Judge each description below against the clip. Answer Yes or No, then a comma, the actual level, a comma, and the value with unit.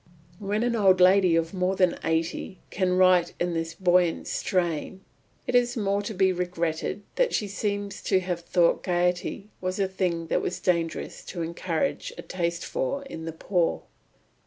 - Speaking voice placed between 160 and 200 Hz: Yes, medium, 185 Hz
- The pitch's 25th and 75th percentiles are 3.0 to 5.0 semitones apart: No, narrow, 2.6 semitones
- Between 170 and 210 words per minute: Yes, average, 175 wpm